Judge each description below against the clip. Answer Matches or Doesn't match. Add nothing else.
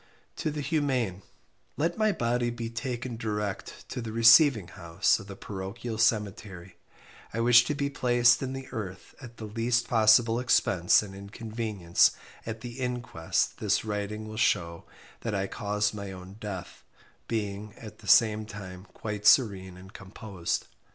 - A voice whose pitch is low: Matches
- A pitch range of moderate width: Matches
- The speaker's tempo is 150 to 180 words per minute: Matches